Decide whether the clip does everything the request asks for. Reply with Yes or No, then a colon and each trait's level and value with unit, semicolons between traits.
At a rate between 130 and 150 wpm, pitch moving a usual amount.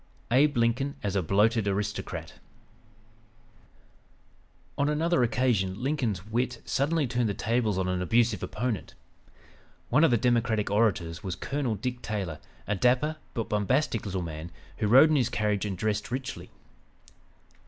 Yes: average, 145 wpm; average, 3.9 semitones